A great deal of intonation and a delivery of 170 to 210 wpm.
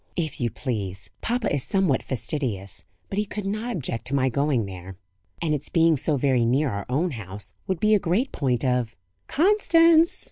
Yes: wide, 8.8 semitones; average, 190 wpm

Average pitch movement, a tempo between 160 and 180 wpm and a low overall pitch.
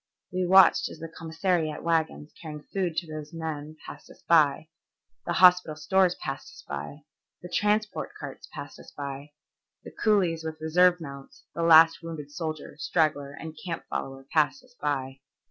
No: average, 3.0 semitones; average, 165 wpm; medium, 160 Hz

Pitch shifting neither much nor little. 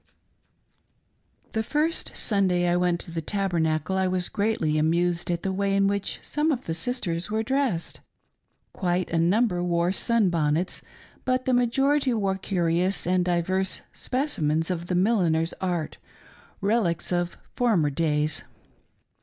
Yes: average, 4.3 semitones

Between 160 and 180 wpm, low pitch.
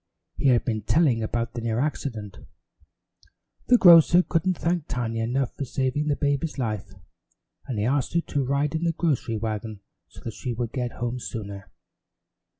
Yes: average, 170 wpm; low, 125 Hz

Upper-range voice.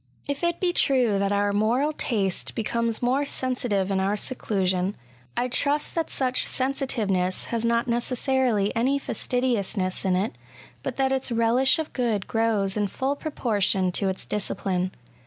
Yes: high, 230 Hz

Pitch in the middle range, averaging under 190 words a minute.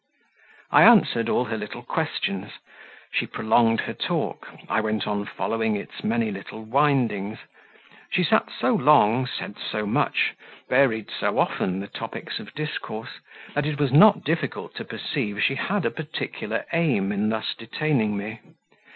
No: low, 115 Hz; average, 150 wpm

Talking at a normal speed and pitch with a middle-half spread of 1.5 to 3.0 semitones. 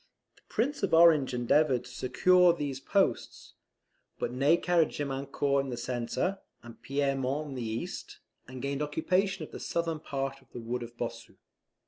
No: average, 165 wpm; average, 4.6 semitones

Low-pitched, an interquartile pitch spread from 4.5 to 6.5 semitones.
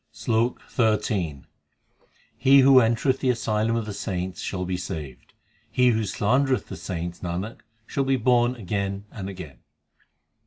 Yes: low, 110 Hz; average, 5.2 semitones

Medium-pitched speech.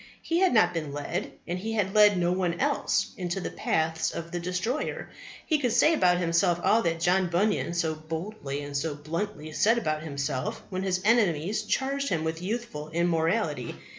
Yes: medium, 175 Hz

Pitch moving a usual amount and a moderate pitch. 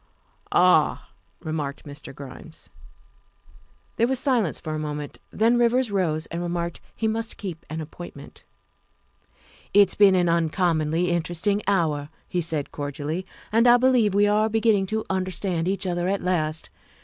Yes: average, 4.7 semitones; medium, 180 Hz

